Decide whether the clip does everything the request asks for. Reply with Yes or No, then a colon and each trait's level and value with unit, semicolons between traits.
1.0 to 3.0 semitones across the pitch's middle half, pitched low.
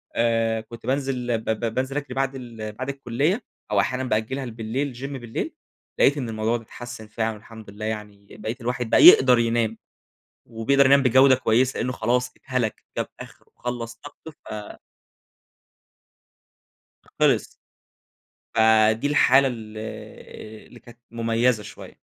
Yes: average, 2.7 semitones; low, 120 Hz